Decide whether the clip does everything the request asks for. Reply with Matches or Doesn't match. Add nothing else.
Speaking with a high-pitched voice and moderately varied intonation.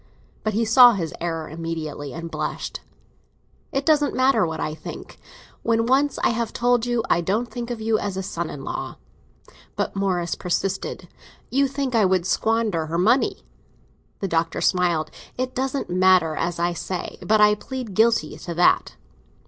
Doesn't match